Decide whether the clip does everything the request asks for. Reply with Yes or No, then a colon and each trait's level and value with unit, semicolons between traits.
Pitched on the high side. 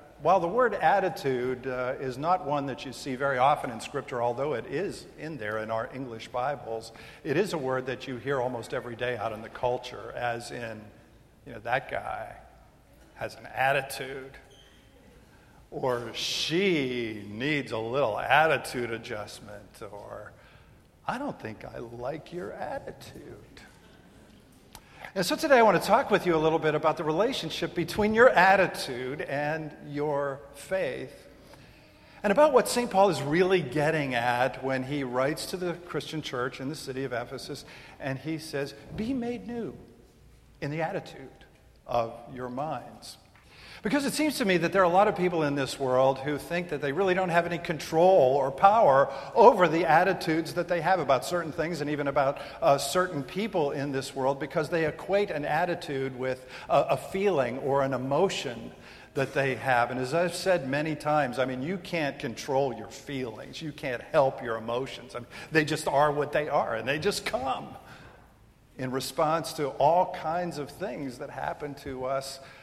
No: medium, 140 Hz